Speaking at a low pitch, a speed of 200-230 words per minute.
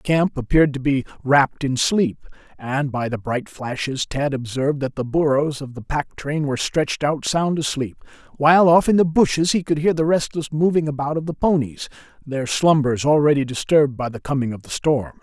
No: medium, 145 Hz; fast, 205 wpm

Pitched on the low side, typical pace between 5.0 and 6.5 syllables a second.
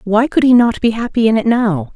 No: high, 220 Hz; 5.4 syllables/s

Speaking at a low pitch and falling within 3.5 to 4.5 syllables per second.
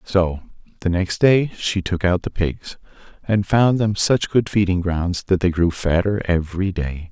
Yes: very low, 95 Hz; 4.3 syllables/s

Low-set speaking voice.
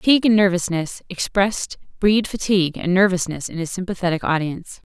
No: medium, 185 Hz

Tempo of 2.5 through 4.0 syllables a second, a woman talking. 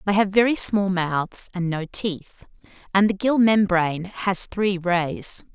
Yes: 3.7 syllables/s; female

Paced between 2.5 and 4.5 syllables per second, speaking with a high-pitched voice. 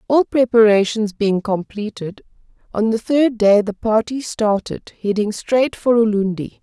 Yes: 4.3 syllables/s; high, 220 Hz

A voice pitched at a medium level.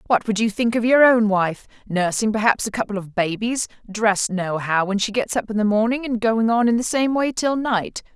No: high, 220 Hz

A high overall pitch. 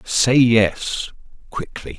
No: low, 110 Hz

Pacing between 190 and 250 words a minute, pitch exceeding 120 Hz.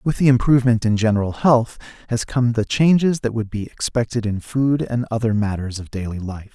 No: average, 200 wpm; low, 115 Hz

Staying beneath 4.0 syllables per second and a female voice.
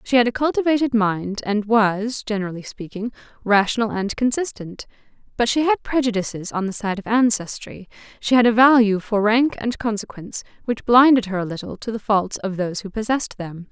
No: 5.5 syllables/s; female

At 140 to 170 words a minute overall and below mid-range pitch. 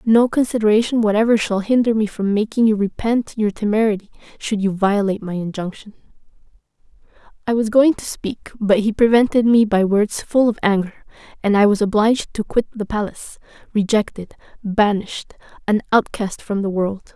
No: average, 160 wpm; high, 215 Hz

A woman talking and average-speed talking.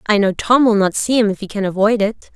No: female; fast, 305 wpm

